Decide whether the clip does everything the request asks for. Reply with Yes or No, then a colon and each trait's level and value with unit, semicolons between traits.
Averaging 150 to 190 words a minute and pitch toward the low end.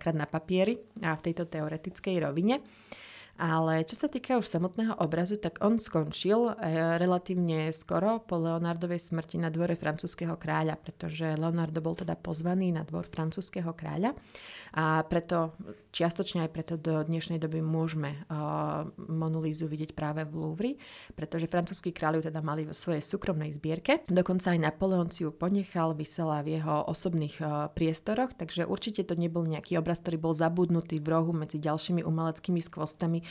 No: average, 160 wpm; medium, 165 Hz